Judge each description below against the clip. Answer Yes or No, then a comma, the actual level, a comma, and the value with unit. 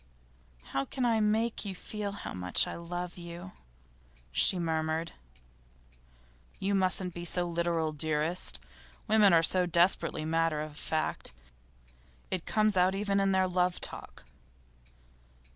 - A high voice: No, medium, 175 Hz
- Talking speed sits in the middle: No, slow, 130 wpm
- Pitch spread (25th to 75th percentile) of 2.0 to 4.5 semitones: Yes, average, 3.1 semitones